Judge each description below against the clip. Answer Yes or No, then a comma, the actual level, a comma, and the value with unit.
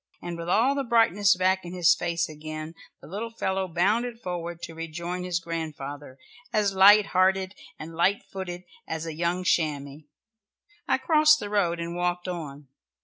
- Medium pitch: Yes, medium, 175 Hz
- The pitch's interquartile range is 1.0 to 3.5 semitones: Yes, average, 2.9 semitones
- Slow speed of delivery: No, average, 165 wpm